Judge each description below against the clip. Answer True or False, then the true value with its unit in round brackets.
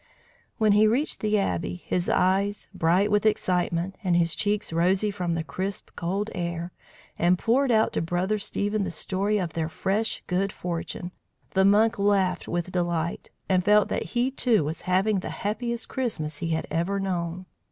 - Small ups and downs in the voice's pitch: False (3.3 semitones)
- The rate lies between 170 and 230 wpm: True (175 wpm)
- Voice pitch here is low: False (190 Hz)